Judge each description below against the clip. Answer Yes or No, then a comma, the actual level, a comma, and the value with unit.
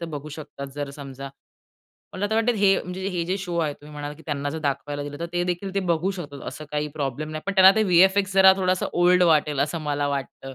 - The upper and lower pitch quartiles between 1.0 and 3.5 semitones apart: No, average, 4.3 semitones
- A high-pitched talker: No, medium, 160 Hz